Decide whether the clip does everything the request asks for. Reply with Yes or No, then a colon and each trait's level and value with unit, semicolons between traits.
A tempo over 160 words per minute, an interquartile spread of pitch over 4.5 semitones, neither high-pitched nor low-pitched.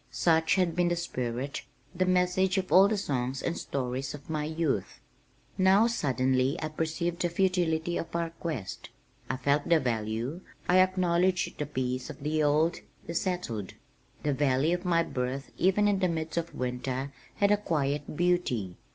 Yes: average, 170 wpm; average, 5.0 semitones; medium, 160 Hz